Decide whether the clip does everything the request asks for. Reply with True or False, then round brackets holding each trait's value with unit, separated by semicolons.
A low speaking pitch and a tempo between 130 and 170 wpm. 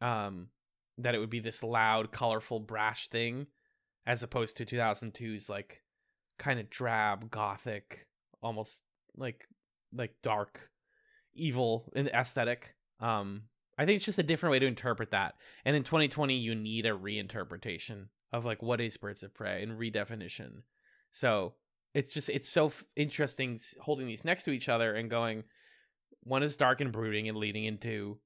True (115 Hz; 160 wpm)